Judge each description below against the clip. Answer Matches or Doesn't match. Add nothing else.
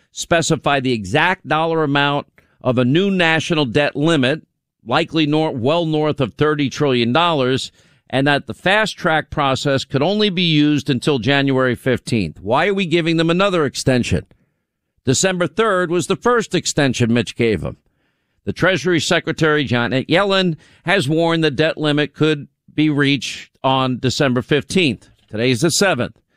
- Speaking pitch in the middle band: Matches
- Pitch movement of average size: Matches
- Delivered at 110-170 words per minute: Matches